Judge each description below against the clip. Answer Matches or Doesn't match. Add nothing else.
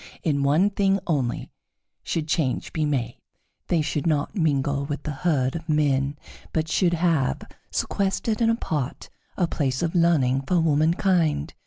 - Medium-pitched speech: Matches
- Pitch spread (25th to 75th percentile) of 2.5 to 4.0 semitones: Matches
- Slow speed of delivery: Doesn't match